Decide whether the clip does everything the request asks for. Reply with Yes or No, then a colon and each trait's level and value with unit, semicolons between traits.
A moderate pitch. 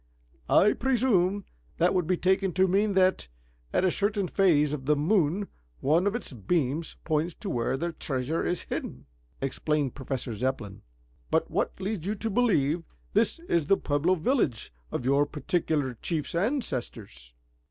Yes: medium, 170 Hz